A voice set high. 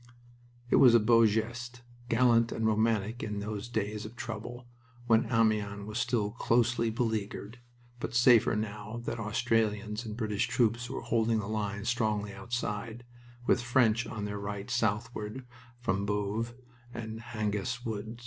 No: low, 110 Hz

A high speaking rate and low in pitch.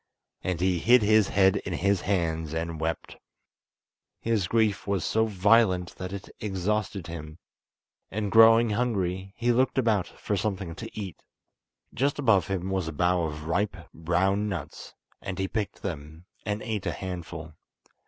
No: average, 155 wpm; very low, 95 Hz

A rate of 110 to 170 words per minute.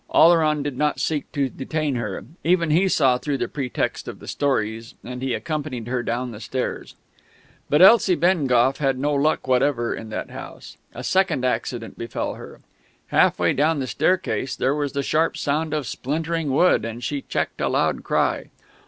No: average, 180 wpm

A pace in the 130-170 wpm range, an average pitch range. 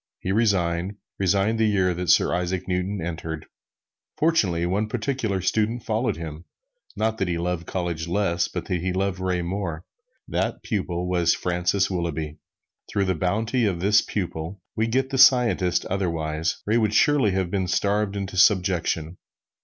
Yes: average, 160 wpm; average, 3.3 semitones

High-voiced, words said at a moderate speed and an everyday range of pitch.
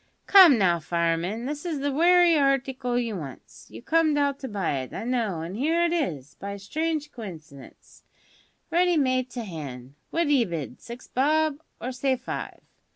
No: very high, 250 Hz; average, 175 wpm; wide, 8.8 semitones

